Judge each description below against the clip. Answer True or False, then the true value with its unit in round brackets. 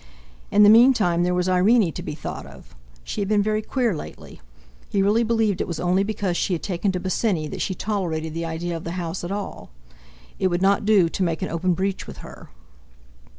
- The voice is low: False (185 Hz)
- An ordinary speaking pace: False (220 wpm)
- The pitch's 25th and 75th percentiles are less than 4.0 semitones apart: True (3.3 semitones)